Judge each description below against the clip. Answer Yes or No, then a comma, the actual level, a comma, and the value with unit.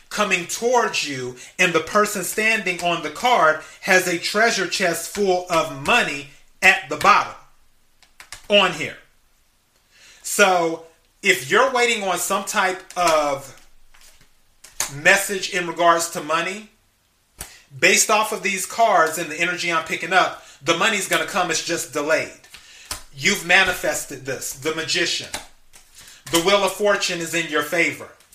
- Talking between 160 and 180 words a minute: No, average, 140 wpm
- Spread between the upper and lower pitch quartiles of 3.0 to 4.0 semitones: Yes, average, 3.7 semitones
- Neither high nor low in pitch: Yes, medium, 175 Hz